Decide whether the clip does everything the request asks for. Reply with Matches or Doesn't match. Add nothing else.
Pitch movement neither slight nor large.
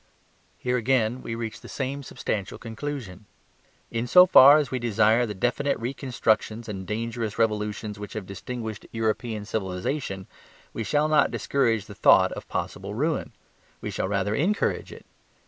Matches